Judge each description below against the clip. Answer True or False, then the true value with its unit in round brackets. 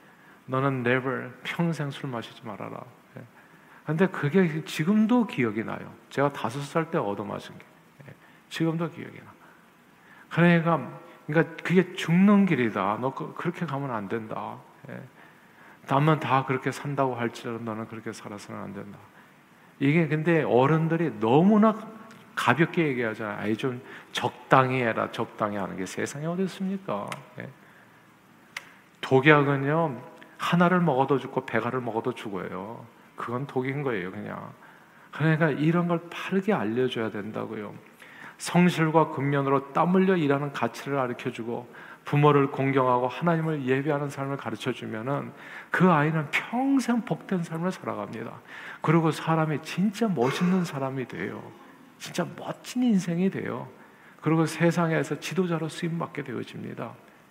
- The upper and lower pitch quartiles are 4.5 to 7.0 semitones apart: True (5.1 semitones)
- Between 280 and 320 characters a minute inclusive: True (305 characters per minute)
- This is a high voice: False (150 Hz)